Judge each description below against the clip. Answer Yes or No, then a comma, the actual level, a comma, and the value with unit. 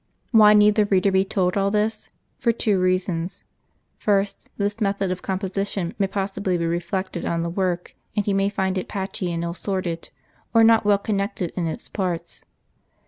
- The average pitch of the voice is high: Yes, high, 195 Hz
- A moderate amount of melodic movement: No, narrow, 2.0 semitones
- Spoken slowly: No, average, 185 wpm